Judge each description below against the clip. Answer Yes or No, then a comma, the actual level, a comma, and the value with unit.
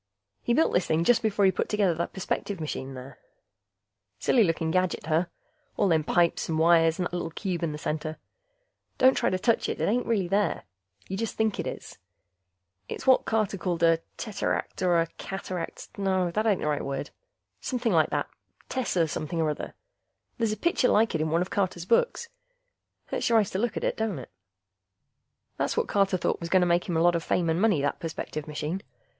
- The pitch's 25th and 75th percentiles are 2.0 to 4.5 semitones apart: Yes, average, 4.2 semitones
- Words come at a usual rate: No, fast, 210 wpm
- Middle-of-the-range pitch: Yes, medium, 180 Hz